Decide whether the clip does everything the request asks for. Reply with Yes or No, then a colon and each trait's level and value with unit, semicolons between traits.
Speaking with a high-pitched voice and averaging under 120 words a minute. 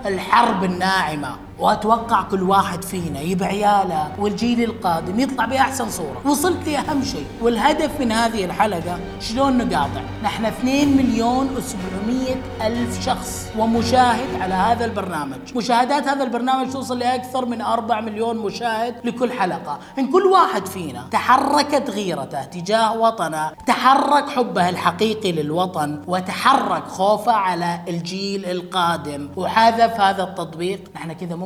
No: high, 220 Hz; average, 125 wpm